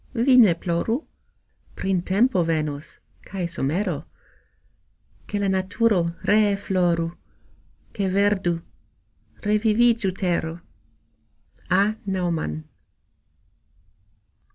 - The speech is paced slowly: Yes, slow, 75 wpm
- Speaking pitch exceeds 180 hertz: Yes, high, 190 Hz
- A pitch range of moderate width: Yes, average, 3.6 semitones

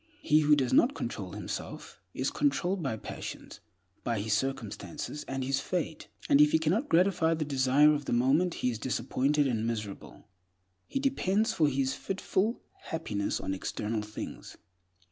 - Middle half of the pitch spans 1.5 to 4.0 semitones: No, wide, 5.4 semitones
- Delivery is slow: No, average, 160 wpm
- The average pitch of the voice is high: No, medium, 145 Hz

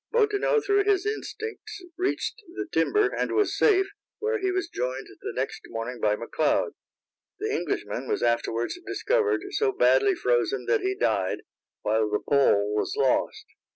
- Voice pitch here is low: No, very high, 390 Hz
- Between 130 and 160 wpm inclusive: Yes, average, 155 wpm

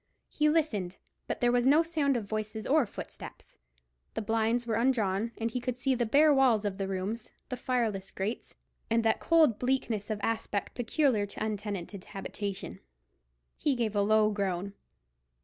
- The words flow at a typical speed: Yes, average, 170 wpm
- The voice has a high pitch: Yes, high, 225 Hz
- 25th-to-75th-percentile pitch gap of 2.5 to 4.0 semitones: Yes, average, 3.7 semitones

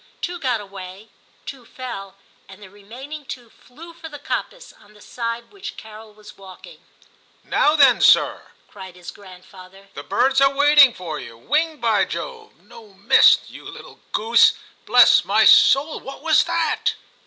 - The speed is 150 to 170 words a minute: Yes, average, 165 wpm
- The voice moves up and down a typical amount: No, wide, 6.6 semitones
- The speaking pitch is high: Yes, high, 235 Hz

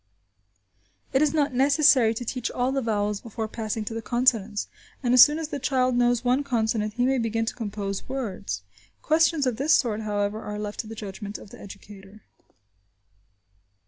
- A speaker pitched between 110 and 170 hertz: No, high, 230 Hz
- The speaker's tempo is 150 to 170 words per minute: No, average, 180 wpm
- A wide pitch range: No, average, 3.7 semitones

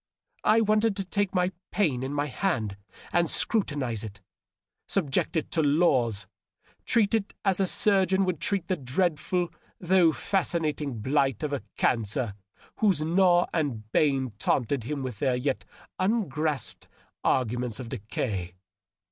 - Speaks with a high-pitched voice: No, medium, 150 Hz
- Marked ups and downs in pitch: Yes, wide, 6.8 semitones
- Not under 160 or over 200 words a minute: No, average, 140 wpm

